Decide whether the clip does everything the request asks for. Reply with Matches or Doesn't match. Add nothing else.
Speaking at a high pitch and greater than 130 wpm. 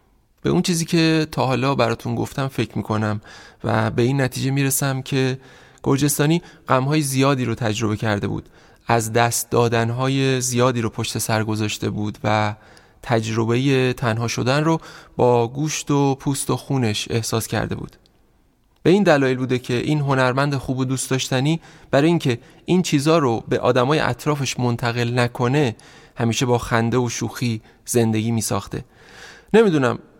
Doesn't match